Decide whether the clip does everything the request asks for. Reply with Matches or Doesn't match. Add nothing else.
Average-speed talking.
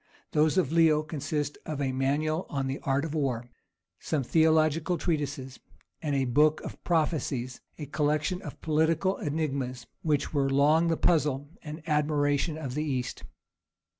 Matches